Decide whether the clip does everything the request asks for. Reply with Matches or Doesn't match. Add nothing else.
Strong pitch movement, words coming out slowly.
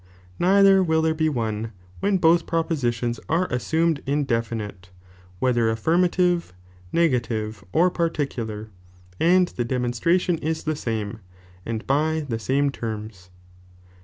Matches